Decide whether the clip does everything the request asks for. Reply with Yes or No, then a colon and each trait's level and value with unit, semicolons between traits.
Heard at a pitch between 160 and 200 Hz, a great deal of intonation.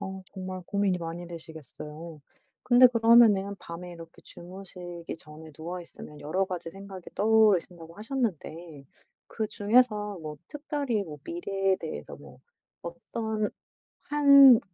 No: high, 190 Hz; average, 4.7 semitones